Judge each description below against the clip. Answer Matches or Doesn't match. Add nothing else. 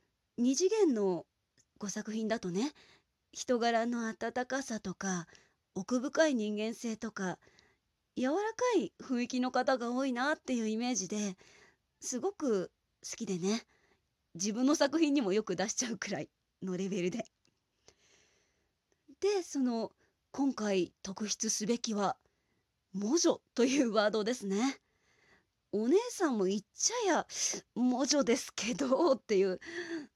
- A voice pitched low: Doesn't match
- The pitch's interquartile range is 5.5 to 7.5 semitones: Doesn't match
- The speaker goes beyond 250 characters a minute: Doesn't match